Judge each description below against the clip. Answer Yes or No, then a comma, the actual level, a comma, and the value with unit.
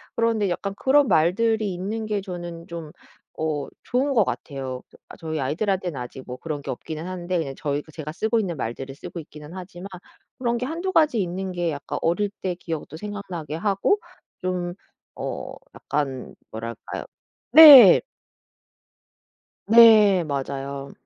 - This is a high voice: No, medium, 175 Hz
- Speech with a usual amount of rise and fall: No, wide, 5.8 semitones